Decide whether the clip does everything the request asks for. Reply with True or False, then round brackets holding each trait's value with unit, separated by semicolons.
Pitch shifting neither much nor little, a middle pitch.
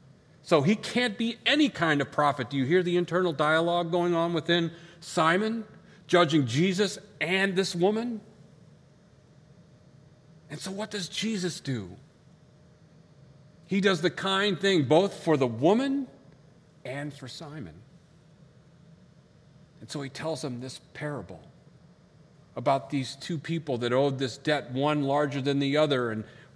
True (3.4 semitones; 155 Hz)